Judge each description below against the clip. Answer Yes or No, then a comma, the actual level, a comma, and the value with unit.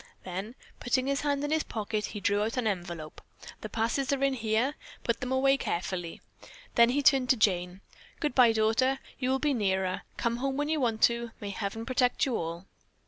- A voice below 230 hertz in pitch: No, high, 235 Hz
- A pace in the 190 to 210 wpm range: Yes, average, 195 wpm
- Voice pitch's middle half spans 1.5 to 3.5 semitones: No, average, 4.6 semitones